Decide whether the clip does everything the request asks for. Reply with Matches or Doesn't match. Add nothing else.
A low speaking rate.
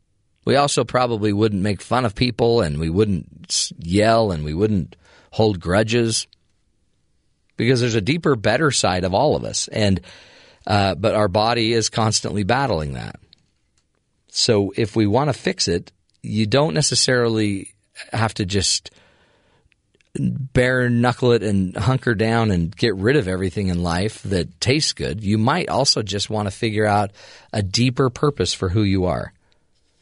Doesn't match